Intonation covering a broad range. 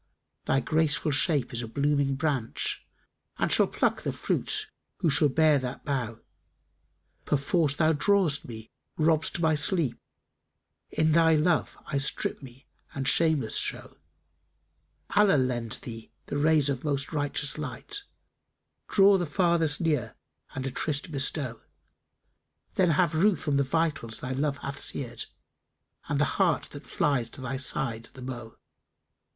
No: average, 3.5 semitones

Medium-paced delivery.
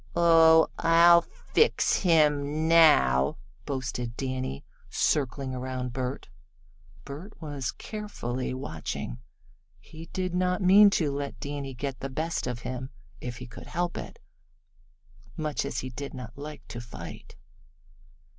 No: slow, 125 wpm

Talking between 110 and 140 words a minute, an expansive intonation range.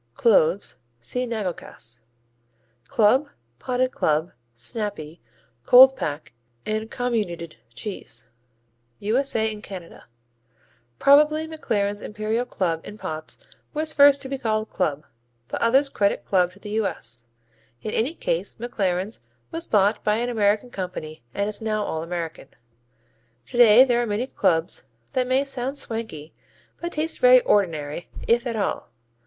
Yes: slow, 135 wpm; wide, 5.8 semitones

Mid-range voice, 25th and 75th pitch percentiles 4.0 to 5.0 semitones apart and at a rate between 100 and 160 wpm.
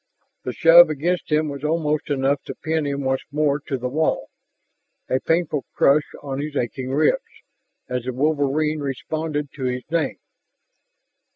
No: medium, 145 Hz; narrow, 2.5 semitones; average, 155 wpm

